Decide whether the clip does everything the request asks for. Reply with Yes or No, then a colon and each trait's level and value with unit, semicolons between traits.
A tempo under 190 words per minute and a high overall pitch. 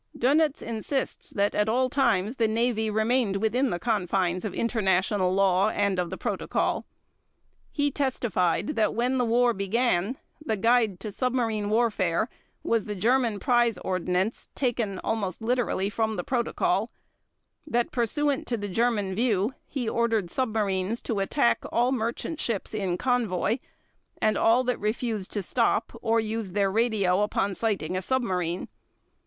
Yes: average, 150 wpm; high, 220 Hz